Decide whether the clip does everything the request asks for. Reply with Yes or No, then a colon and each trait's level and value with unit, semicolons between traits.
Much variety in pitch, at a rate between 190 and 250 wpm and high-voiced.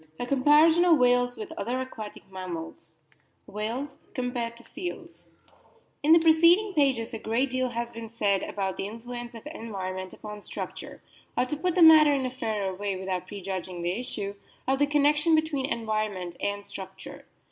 No: wide, 6.3 semitones; average, 175 wpm; high, 240 Hz